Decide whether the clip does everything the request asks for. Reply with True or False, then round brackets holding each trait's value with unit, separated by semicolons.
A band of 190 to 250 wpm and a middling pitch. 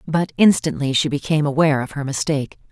False (175 wpm; 150 Hz)